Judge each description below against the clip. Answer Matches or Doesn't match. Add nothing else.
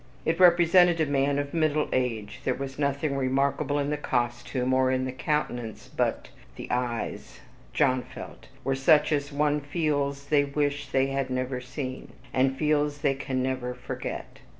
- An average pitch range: Doesn't match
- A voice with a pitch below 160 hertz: Matches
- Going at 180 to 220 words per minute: Doesn't match